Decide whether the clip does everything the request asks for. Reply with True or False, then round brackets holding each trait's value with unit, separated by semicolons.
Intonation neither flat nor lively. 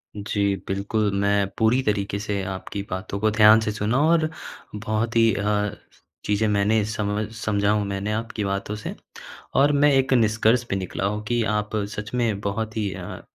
False (1.7 semitones)